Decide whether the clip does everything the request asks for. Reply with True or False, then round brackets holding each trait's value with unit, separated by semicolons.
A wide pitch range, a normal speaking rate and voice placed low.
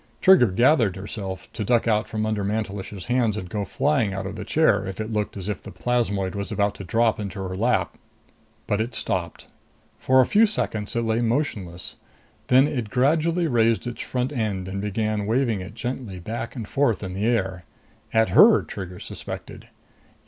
False (3.8 semitones; 185 wpm; 110 Hz)